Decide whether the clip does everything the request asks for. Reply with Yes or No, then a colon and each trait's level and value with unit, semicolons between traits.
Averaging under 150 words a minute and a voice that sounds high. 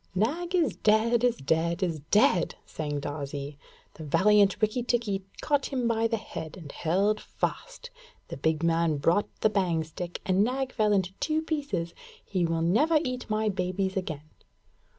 No: average, 165 wpm; high, 195 Hz